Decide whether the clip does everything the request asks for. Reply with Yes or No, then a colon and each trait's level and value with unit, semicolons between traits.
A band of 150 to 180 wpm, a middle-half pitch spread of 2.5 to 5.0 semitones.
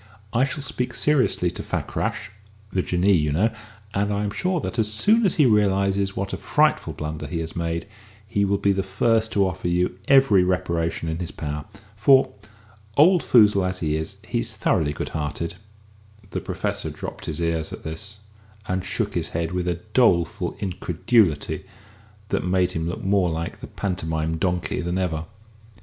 Yes: average, 175 wpm; average, 3.8 semitones